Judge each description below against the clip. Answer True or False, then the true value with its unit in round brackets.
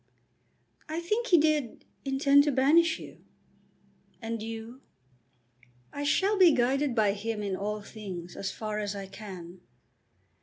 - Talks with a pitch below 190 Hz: False (230 Hz)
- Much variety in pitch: True (6.0 semitones)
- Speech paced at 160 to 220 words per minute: False (140 wpm)